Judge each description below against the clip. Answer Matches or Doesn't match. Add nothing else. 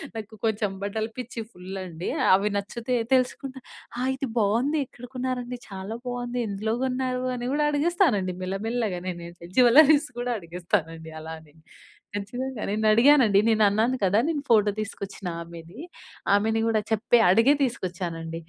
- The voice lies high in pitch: Matches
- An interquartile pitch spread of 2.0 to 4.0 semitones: Doesn't match